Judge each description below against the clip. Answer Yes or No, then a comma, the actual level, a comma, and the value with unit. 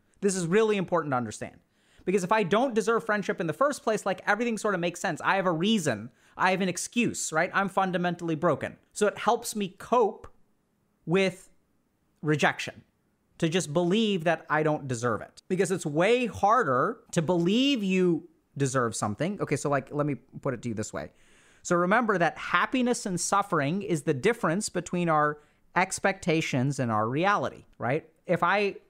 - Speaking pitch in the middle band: Yes, medium, 175 Hz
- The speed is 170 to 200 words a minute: Yes, average, 180 wpm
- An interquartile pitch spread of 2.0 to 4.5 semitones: No, average, 5.2 semitones